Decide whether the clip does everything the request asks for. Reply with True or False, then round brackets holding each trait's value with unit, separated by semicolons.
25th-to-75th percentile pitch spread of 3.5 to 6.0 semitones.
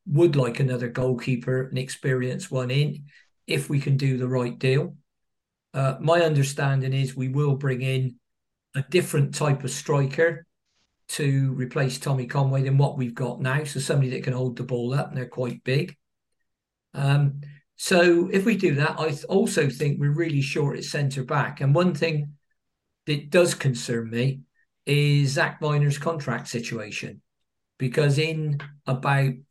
False (2.9 semitones)